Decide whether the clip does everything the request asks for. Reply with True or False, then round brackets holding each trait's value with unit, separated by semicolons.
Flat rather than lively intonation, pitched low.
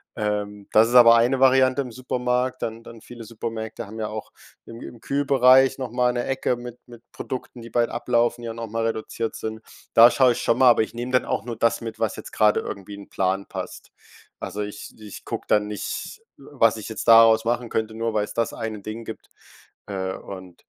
True (2.1 semitones; 115 Hz)